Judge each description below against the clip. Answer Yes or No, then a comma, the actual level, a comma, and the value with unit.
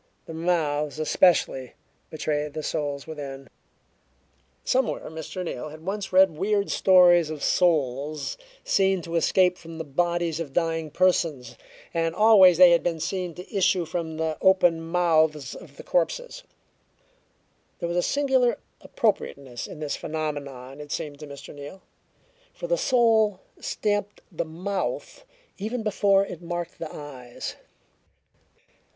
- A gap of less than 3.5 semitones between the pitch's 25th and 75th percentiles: No, average, 4.0 semitones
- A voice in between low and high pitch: Yes, medium, 170 Hz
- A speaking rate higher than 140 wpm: No, slow, 135 wpm